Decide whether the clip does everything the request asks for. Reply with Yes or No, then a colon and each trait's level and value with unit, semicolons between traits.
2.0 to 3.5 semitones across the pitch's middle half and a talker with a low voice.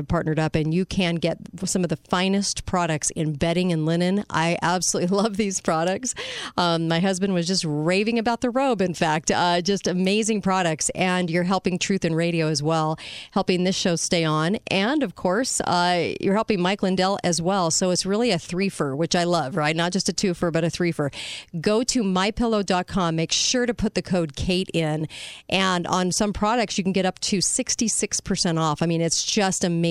No: average, 3.0 semitones; medium, 180 Hz